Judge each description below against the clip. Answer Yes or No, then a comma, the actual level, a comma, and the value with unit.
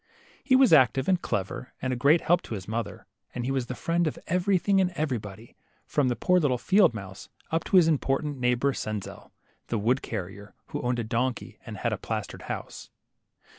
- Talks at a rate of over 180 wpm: Yes, average, 200 wpm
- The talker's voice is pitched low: Yes, low, 130 Hz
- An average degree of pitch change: No, wide, 6.4 semitones